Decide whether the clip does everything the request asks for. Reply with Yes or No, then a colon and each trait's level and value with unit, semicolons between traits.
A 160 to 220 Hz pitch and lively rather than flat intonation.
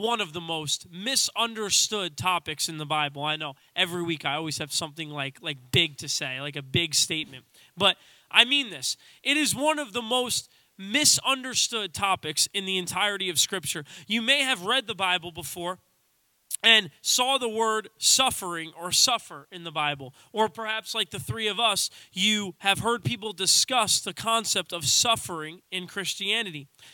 Yes: medium, 185 Hz; wide, 6.3 semitones